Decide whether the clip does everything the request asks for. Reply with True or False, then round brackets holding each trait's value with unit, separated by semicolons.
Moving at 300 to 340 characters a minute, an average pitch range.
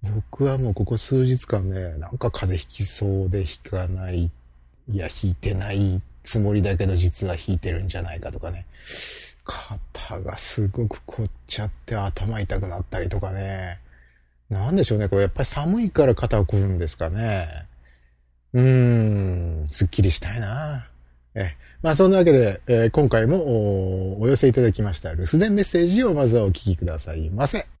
True (335 characters per minute; 4.5 semitones)